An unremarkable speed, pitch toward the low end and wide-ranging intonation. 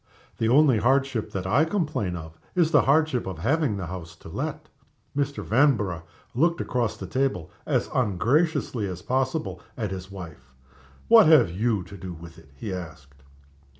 Yes: average, 165 wpm; low, 110 Hz; wide, 7.4 semitones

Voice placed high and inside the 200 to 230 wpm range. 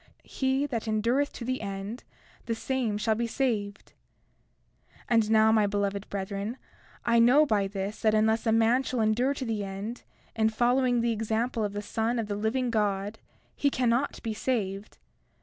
No: high, 225 Hz; average, 175 wpm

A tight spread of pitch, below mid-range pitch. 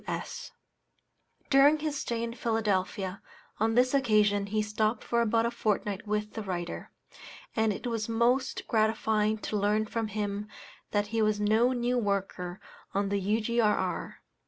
No: narrow, 2.2 semitones; high, 215 Hz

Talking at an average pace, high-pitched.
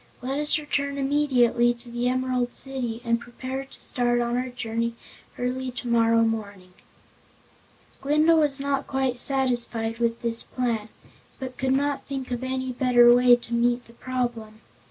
Yes: average, 155 wpm; high, 245 Hz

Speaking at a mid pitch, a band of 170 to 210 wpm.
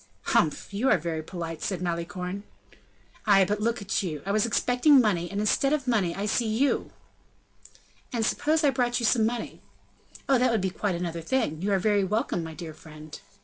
No: high, 200 Hz; average, 190 wpm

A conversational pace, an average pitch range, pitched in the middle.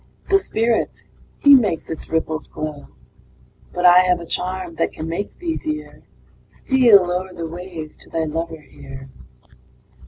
Yes: average, 150 wpm; average, 4.0 semitones; medium, 175 Hz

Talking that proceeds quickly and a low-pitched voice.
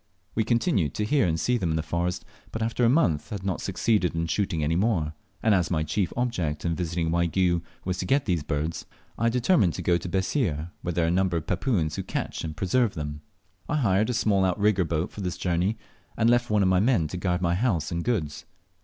Yes: fast, 235 wpm; very low, 90 Hz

